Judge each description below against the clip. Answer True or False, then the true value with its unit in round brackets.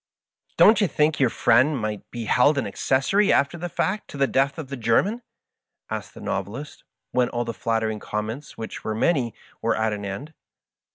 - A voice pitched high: False (125 Hz)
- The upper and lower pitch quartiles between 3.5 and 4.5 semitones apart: False (5.2 semitones)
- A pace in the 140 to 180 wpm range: False (195 wpm)